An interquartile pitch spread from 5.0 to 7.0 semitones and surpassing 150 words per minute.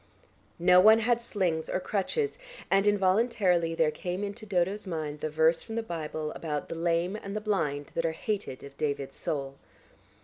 No: average, 4.6 semitones; average, 175 wpm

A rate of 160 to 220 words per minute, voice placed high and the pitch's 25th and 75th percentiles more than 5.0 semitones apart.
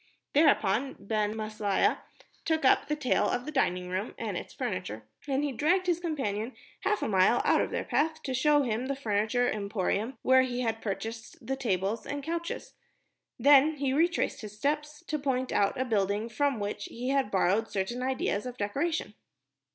Yes: average, 180 wpm; very high, 250 Hz; wide, 5.4 semitones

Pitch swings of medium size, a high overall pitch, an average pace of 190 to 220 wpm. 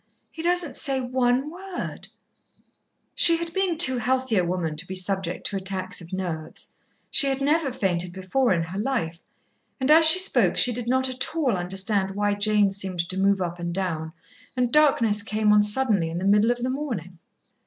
No: wide, 6.1 semitones; high, 210 Hz; average, 195 wpm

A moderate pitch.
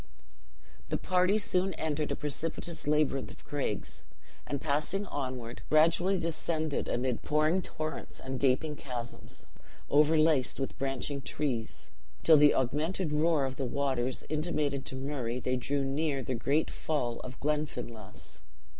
Yes: medium, 145 Hz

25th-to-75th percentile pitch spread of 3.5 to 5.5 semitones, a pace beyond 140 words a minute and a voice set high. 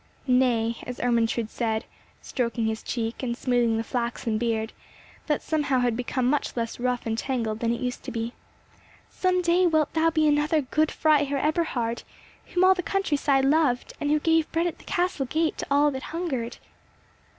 Yes: average, 4.9 semitones; average, 185 wpm; very high, 260 Hz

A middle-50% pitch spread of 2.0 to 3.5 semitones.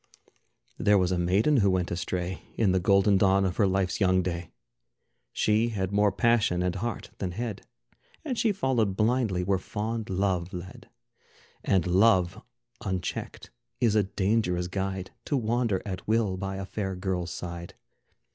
Yes: average, 2.8 semitones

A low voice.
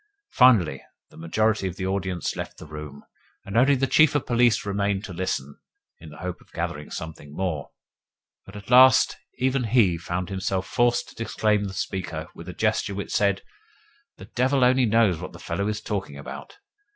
Yes: low, 100 Hz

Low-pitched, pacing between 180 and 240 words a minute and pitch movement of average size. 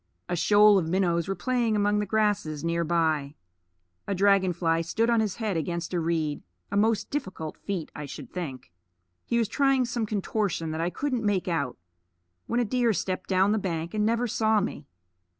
No: high, 195 Hz; average, 190 wpm; average, 4.6 semitones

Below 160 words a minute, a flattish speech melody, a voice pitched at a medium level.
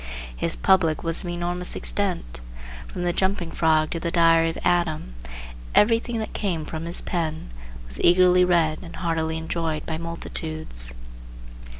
Yes: average, 145 wpm; narrow, 1.9 semitones; medium, 165 Hz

